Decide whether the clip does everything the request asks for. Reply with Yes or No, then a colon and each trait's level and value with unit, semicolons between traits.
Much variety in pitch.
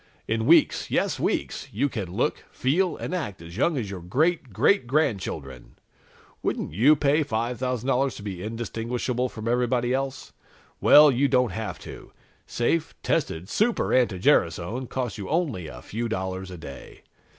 Yes: wide, 5.7 semitones